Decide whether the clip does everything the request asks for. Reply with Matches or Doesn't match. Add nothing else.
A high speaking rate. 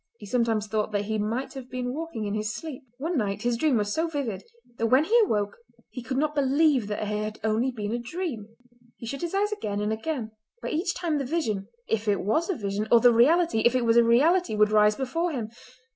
Matches